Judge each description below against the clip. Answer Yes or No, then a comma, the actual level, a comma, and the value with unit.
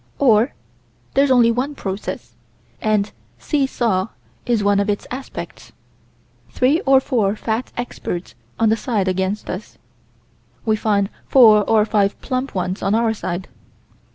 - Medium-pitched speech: No, high, 220 Hz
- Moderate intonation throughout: Yes, average, 3.7 semitones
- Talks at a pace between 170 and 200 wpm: No, average, 140 wpm